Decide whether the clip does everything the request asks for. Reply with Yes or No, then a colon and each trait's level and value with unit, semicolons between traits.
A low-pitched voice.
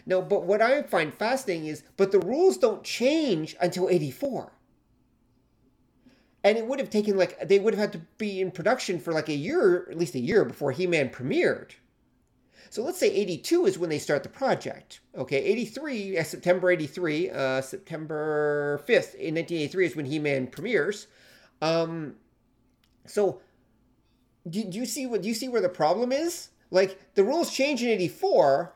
No: medium, 180 Hz